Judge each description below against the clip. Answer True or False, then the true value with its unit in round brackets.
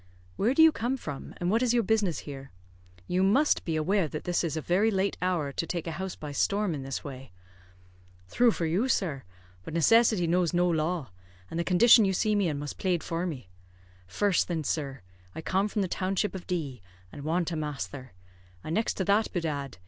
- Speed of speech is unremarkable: False (210 wpm)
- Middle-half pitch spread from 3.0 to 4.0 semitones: False (4.7 semitones)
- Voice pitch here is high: False (175 Hz)